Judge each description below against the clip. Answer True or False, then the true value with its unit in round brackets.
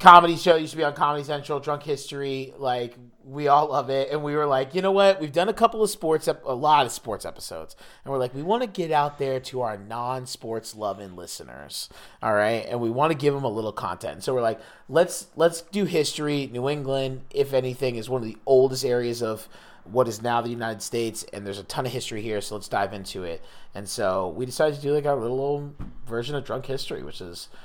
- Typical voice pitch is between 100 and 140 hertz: True (135 Hz)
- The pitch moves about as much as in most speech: True (4.1 semitones)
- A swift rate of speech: True (240 wpm)